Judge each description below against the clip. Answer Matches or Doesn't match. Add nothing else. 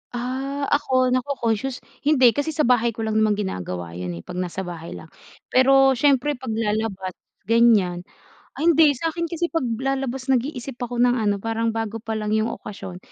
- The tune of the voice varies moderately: Matches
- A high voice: Matches